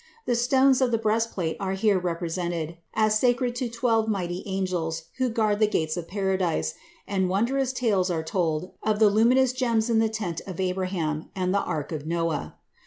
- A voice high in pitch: Yes, high, 195 Hz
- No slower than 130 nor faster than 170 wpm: No, average, 180 wpm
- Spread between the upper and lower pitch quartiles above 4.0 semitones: Yes, average, 4.7 semitones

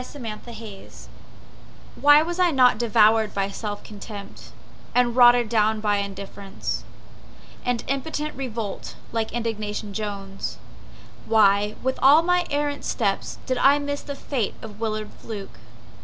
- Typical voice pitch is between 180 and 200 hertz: No, high, 225 Hz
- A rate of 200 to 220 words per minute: No, slow, 135 wpm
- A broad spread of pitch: No, average, 4.2 semitones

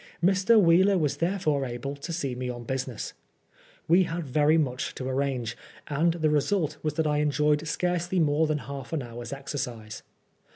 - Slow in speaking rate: No, average, 165 wpm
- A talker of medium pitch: Yes, medium, 150 Hz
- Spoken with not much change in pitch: No, average, 4.0 semitones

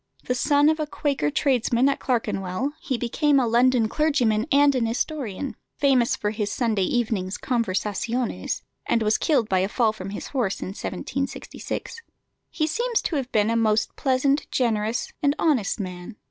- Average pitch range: Yes, average, 4.7 semitones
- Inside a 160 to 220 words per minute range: Yes, average, 165 wpm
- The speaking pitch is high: Yes, high, 240 Hz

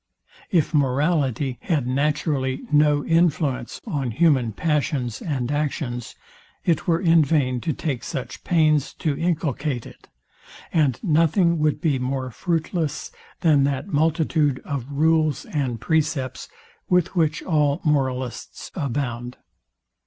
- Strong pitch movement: No, average, 3.5 semitones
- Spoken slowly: Yes, slow, 120 wpm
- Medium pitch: Yes, medium, 150 Hz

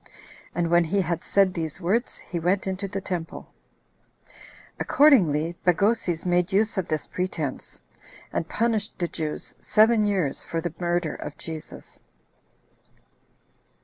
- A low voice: No, medium, 175 Hz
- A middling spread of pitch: Yes, average, 3.2 semitones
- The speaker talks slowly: Yes, slow, 130 wpm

